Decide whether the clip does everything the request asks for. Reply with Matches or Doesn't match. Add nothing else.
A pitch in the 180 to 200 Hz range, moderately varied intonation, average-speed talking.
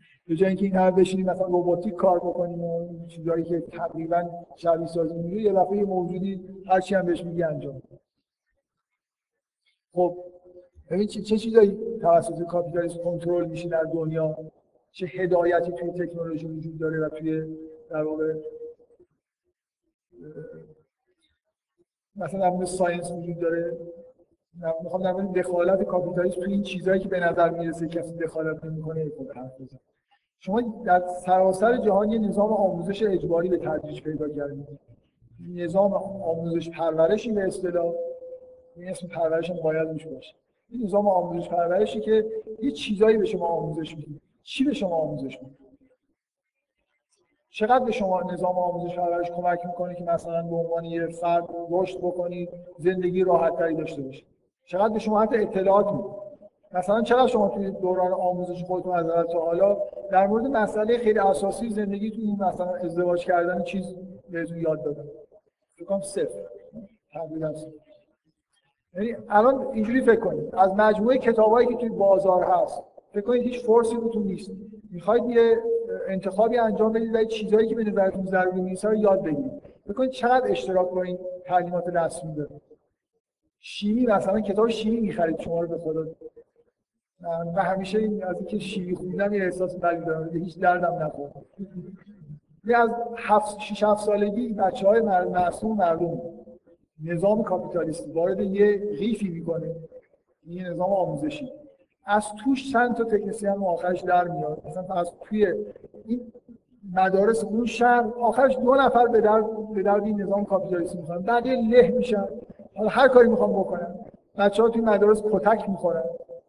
Matches